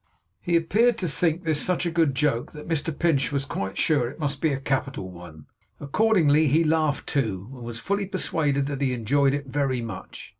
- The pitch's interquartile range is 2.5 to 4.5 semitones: Yes, average, 3.9 semitones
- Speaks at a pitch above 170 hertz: No, medium, 145 Hz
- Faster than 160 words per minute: Yes, average, 200 wpm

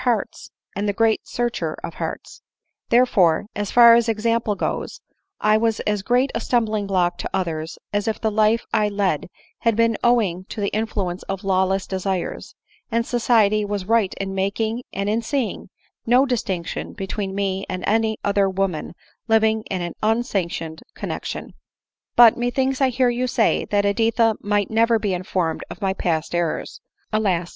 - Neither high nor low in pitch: No, high, 210 Hz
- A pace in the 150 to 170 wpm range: Yes, average, 165 wpm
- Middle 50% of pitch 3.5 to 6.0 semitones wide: No, average, 3.1 semitones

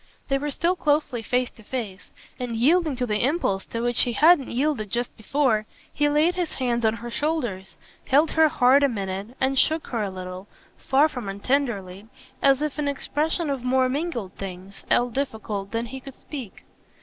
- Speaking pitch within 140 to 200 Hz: No, very high, 250 Hz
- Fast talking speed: No, average, 185 wpm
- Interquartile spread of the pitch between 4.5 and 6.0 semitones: Yes, average, 5.1 semitones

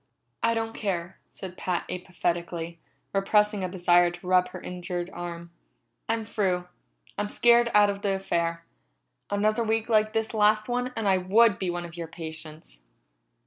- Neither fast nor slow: Yes, average, 160 wpm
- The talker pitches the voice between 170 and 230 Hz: Yes, medium, 185 Hz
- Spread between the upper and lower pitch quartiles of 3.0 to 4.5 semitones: Yes, average, 3.6 semitones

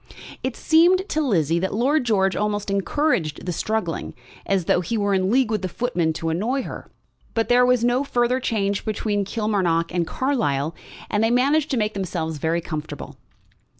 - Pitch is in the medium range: No, high, 210 Hz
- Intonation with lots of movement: Yes, wide, 6.0 semitones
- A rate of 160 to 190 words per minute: Yes, average, 180 wpm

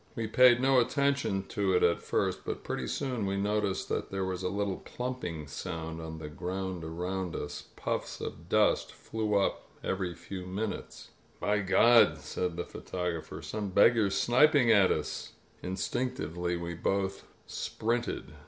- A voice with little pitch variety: No, average, 4.0 semitones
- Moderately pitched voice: No, very low, 95 Hz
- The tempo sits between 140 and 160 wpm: Yes, average, 155 wpm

